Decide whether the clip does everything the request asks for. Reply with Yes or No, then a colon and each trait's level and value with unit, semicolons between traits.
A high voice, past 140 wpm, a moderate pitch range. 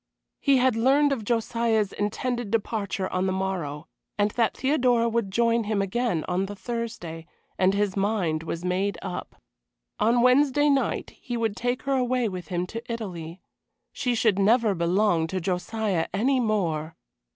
Yes: high, 210 Hz; average, 160 wpm; average, 4.3 semitones